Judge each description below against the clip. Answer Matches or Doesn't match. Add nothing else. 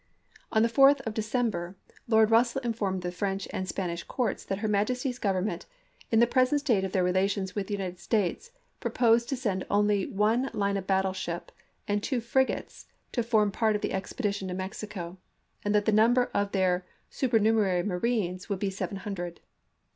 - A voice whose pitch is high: Matches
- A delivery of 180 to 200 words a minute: Matches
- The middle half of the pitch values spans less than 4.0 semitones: Matches